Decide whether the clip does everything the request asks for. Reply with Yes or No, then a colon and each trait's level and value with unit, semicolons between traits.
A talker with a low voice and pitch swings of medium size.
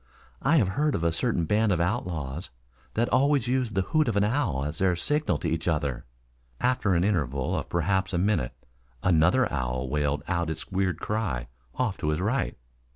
No: very low, 90 Hz; wide, 6.3 semitones